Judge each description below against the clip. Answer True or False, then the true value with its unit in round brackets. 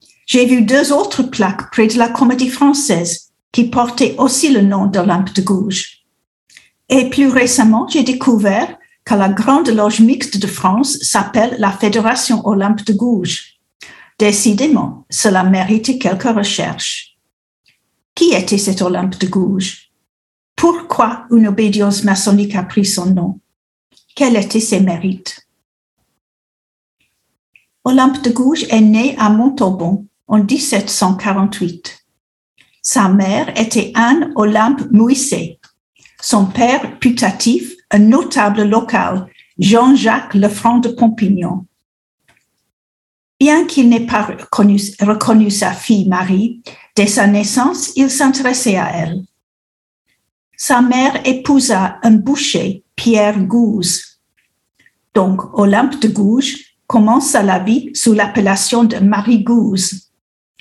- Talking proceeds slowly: True (115 wpm)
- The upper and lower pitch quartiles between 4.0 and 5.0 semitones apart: True (4.4 semitones)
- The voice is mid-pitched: False (220 Hz)